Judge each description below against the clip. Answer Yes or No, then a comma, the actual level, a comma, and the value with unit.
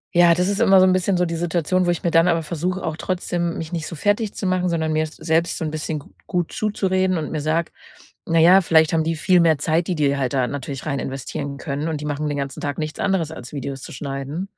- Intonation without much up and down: No, average, 3.1 semitones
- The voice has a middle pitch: Yes, medium, 165 Hz